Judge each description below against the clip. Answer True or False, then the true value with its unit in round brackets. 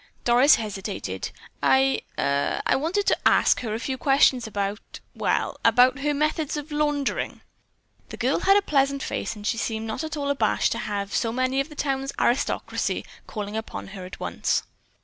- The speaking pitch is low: False (265 Hz)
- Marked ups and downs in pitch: False (4.6 semitones)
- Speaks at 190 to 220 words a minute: False (165 wpm)